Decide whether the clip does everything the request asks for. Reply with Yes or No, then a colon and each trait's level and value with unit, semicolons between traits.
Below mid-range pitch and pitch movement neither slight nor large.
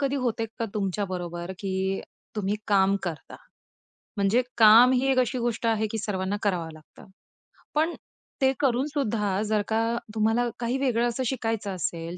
No: high, 220 Hz; average, 4.0 semitones